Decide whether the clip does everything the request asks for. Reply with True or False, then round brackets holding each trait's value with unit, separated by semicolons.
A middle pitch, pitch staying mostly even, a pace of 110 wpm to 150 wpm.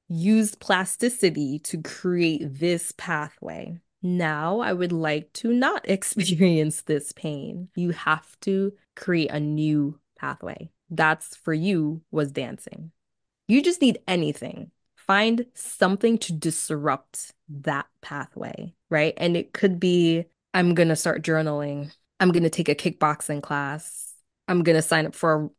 False (170 Hz; 3.7 semitones; 145 wpm)